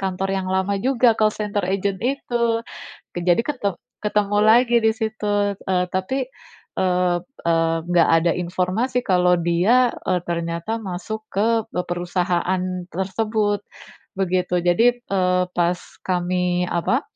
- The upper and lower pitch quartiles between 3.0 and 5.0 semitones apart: Yes, average, 3.4 semitones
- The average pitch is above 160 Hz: Yes, medium, 185 Hz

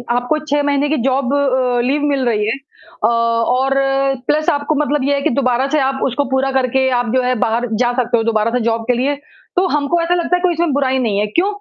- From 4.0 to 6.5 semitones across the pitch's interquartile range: No, average, 3.1 semitones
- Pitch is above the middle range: Yes, very high, 265 Hz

